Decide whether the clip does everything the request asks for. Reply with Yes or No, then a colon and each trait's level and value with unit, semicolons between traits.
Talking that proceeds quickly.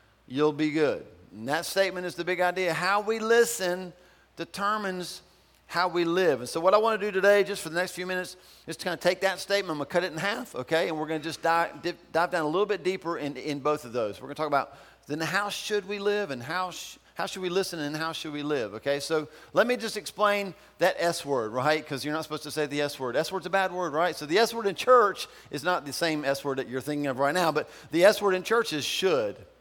Yes: fast, 280 wpm